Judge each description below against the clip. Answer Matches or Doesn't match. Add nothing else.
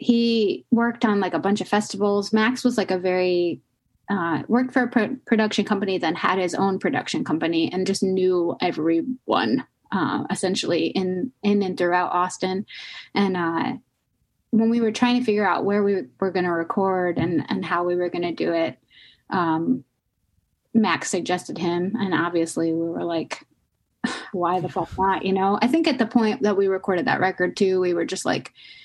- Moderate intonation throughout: Matches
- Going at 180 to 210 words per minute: Matches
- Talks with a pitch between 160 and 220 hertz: Matches